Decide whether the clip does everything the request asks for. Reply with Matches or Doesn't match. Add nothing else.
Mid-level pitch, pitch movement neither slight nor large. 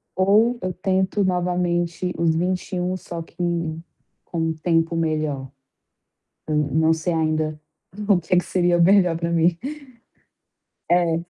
Doesn't match